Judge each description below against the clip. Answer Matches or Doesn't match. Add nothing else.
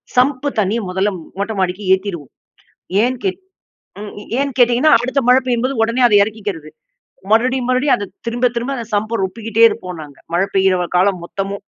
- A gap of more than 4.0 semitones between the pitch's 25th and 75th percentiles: Matches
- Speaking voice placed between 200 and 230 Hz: Matches